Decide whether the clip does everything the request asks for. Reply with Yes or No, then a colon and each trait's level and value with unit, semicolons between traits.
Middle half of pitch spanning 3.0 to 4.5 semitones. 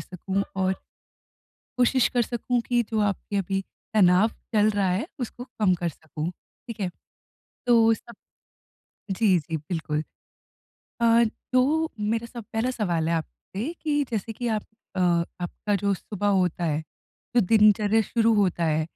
Yes: average, 4.1 semitones